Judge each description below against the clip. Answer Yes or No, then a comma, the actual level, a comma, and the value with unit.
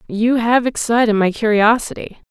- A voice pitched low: No, high, 225 Hz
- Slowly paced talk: Yes, slow, 130 wpm